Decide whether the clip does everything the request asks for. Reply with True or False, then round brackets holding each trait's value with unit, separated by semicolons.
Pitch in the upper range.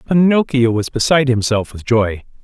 False (125 Hz)